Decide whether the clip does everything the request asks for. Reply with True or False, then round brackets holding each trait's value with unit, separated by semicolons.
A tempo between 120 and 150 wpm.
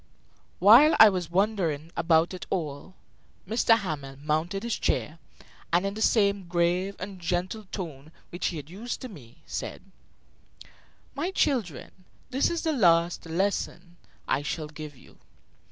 True (145 wpm)